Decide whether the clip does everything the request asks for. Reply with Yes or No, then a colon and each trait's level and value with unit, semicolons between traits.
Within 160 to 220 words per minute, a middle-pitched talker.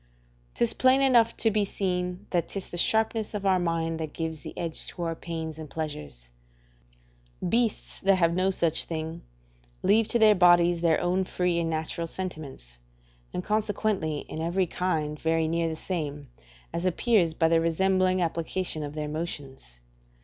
Yes: average, 165 wpm; medium, 170 Hz